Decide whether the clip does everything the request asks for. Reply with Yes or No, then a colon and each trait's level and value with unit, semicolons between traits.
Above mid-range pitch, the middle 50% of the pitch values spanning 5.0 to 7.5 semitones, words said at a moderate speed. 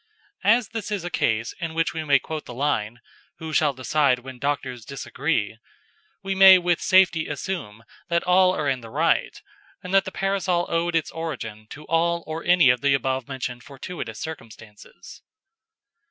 No: medium, 155 Hz; wide, 5.5 semitones; average, 170 wpm